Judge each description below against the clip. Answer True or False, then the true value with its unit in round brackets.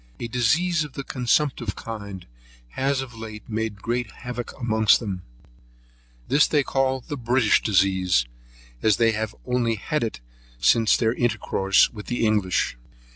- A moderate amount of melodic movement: True (3.1 semitones)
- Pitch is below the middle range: True (115 Hz)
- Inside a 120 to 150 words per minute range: True (145 wpm)